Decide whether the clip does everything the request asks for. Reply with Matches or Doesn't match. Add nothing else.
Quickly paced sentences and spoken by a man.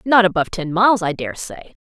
Doesn't match